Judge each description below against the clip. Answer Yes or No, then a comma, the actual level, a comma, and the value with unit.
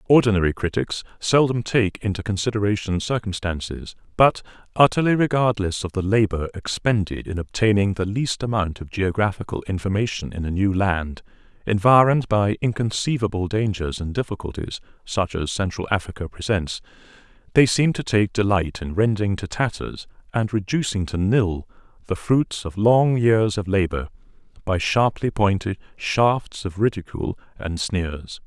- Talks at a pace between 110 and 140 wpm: Yes, slow, 135 wpm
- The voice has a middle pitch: No, low, 100 Hz